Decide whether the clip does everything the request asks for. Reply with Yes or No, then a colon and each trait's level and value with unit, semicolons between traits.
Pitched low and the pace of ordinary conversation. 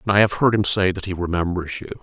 No: very low, 95 Hz; fast, 295 wpm